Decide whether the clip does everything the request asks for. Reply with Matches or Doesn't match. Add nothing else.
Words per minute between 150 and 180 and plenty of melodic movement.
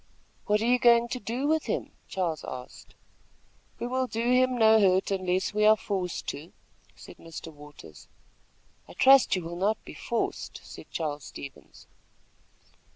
Matches